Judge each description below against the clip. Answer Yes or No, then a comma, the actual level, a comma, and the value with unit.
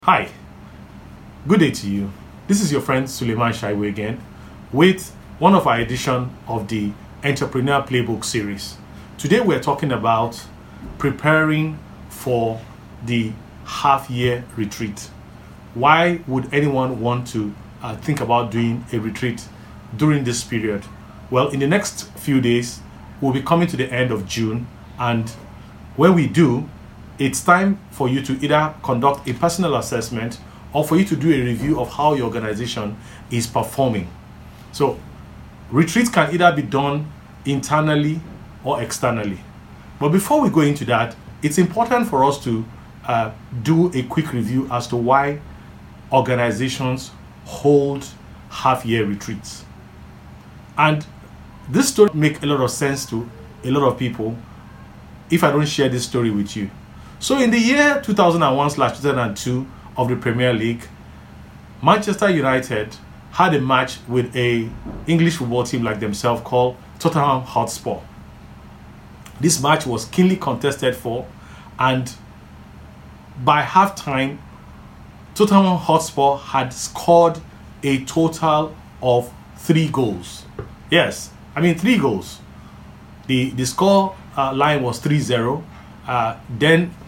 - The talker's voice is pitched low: Yes, low, 125 Hz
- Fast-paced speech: No, slow, 135 wpm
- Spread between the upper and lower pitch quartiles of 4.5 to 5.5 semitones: Yes, average, 5.2 semitones